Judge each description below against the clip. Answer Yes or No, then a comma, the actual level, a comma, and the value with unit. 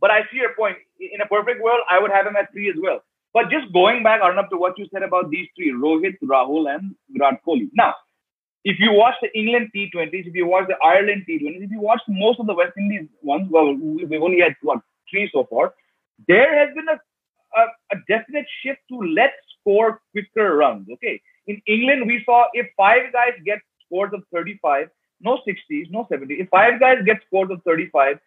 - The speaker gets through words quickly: Yes, fast, 210 wpm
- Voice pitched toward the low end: No, high, 210 Hz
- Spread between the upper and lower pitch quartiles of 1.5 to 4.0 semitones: No, average, 4.8 semitones